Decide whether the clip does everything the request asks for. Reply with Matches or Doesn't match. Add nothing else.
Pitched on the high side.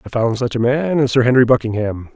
Doesn't match